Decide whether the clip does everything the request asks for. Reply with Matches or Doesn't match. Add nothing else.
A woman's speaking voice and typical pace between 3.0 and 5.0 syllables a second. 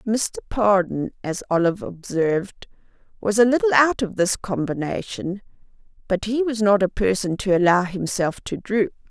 Matches